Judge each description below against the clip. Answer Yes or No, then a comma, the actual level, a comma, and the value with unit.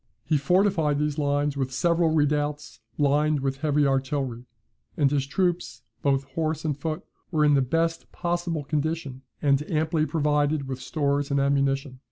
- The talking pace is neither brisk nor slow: Yes, average, 155 wpm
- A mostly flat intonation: Yes, narrow, 2.3 semitones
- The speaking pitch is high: No, medium, 145 Hz